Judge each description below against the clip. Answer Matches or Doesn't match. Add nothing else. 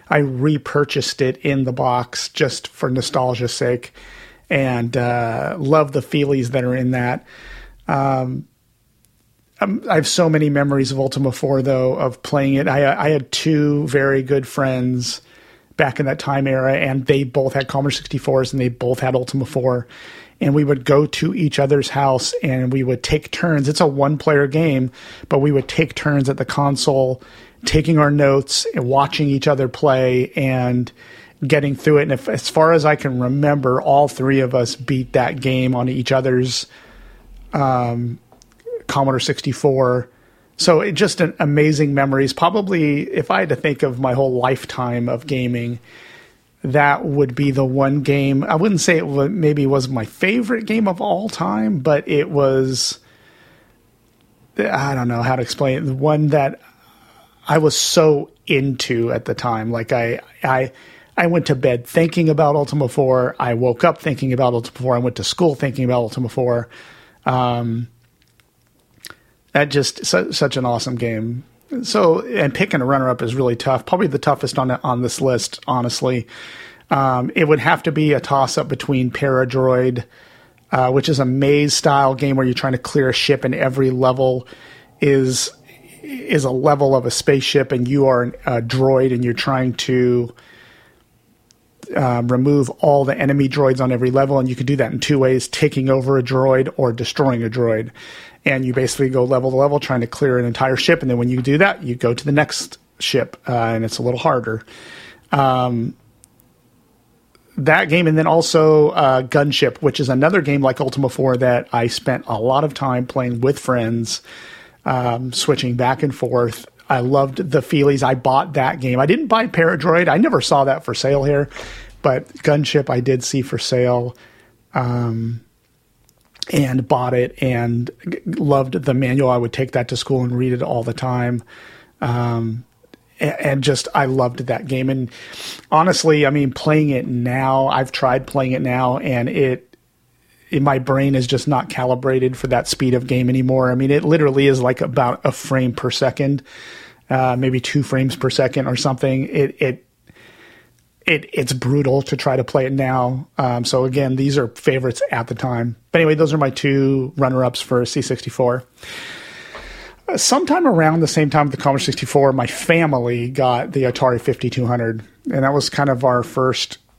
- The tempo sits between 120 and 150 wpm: Doesn't match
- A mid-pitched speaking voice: Doesn't match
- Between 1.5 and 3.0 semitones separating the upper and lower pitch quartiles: Matches